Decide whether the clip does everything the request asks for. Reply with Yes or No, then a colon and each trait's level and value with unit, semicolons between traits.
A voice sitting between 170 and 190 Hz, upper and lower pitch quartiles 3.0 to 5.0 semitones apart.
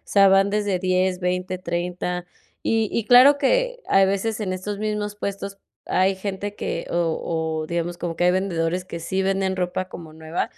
No: medium, 185 Hz; narrow, 2.4 semitones